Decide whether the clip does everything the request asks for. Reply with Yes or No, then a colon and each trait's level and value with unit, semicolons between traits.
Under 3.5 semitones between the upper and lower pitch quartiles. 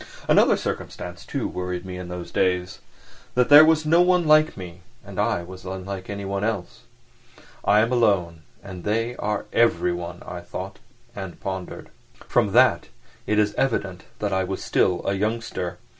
No: average, 4.0 semitones